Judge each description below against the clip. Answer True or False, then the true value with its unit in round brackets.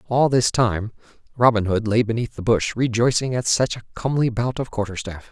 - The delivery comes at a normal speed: True (190 wpm)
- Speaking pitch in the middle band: False (115 Hz)